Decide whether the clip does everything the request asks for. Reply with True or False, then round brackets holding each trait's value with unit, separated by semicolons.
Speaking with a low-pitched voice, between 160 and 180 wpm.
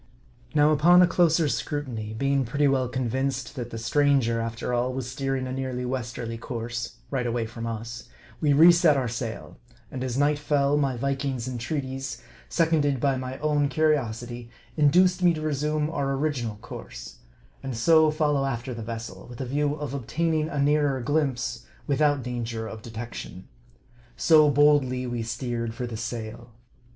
True (130 Hz; 165 wpm)